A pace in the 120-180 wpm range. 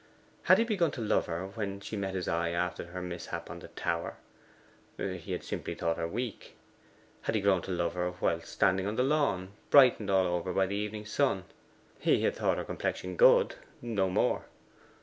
No: average, 195 wpm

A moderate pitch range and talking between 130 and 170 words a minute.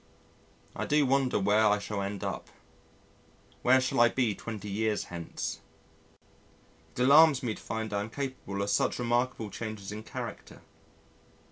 Yes: average, 3.8 semitones; average, 150 wpm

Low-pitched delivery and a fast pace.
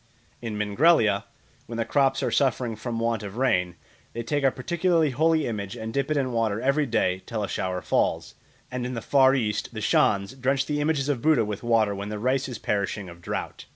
Yes: low, 120 Hz; fast, 215 wpm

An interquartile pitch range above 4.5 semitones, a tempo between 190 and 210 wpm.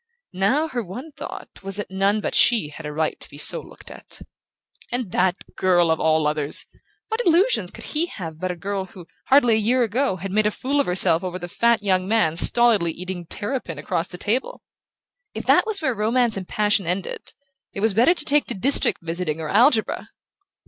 Yes: wide, 5.5 semitones; fast, 205 wpm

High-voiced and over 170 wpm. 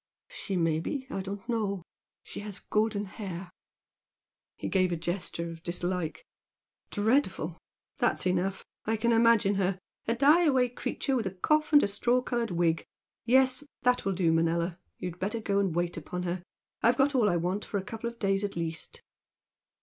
Yes: high, 200 Hz; average, 180 wpm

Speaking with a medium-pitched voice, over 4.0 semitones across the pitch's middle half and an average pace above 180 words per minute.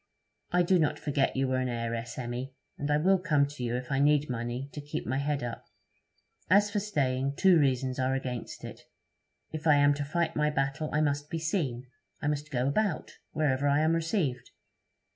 No: medium, 145 Hz; average, 3.1 semitones; average, 200 wpm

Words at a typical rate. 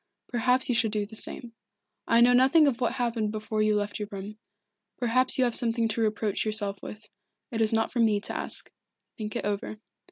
No: fast, 210 wpm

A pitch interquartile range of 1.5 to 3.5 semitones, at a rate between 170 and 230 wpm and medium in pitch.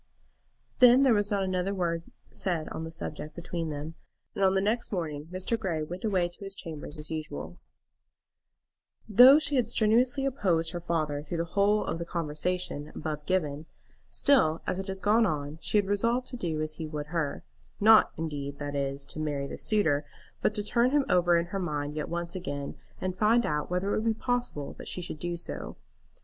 No: average, 5.2 semitones; average, 200 wpm; medium, 175 Hz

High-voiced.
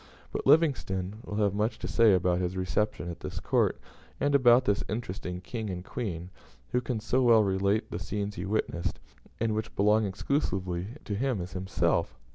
No: low, 105 Hz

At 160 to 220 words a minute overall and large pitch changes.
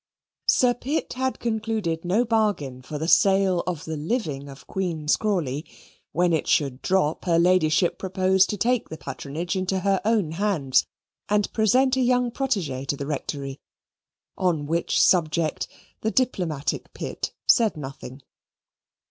No: average, 145 wpm; wide, 5.8 semitones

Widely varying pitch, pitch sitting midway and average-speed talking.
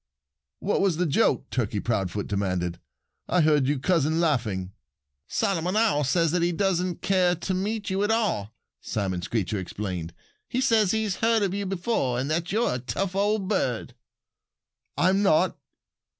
Yes: wide, 8.9 semitones; medium, 170 Hz; average, 165 wpm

